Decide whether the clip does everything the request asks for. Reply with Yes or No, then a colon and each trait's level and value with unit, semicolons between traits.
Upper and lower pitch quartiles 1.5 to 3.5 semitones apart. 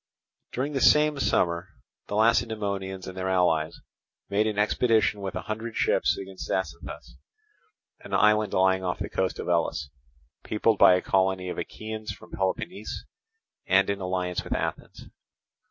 Yes: average, 2.7 semitones